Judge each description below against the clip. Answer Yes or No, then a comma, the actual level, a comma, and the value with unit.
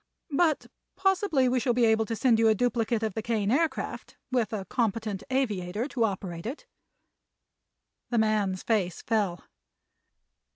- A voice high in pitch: Yes, high, 225 Hz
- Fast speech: No, average, 150 wpm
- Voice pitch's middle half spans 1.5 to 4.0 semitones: Yes, average, 3.4 semitones